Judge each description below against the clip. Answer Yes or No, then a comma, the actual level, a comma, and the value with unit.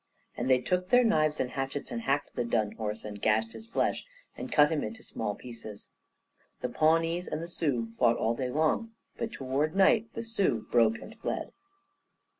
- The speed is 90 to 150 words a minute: No, average, 185 wpm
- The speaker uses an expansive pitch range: Yes, wide, 6.9 semitones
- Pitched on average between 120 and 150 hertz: Yes, low, 135 Hz